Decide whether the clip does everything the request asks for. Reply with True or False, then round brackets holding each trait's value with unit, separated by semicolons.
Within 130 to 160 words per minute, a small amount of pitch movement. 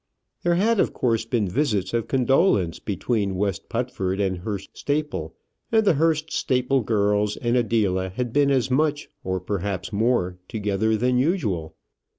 False (155 wpm; 5.4 semitones)